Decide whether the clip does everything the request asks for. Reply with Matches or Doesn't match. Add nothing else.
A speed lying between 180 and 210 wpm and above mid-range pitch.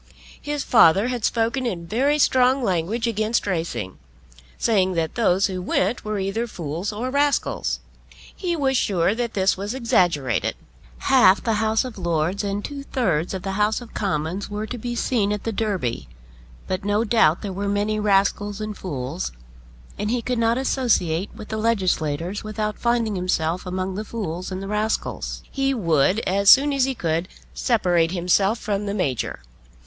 Doesn't match